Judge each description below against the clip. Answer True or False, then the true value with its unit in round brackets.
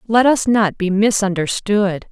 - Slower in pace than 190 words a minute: True (140 wpm)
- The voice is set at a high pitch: True (205 Hz)